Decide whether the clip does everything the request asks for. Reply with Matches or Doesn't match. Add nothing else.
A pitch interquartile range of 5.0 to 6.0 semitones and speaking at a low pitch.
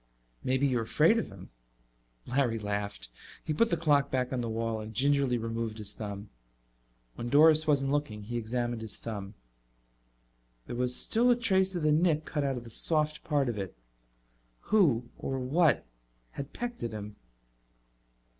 Matches